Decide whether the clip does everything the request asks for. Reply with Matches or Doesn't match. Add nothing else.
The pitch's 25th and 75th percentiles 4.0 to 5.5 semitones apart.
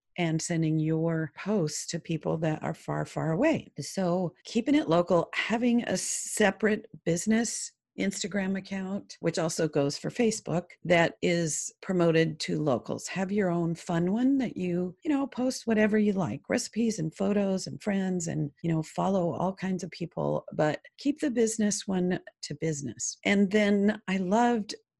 Matches